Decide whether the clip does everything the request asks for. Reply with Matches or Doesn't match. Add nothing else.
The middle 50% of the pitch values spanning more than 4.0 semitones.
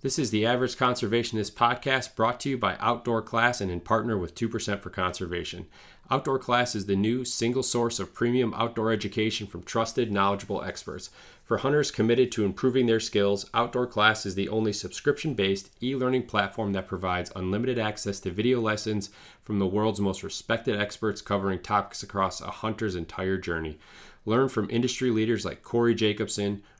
Doesn't match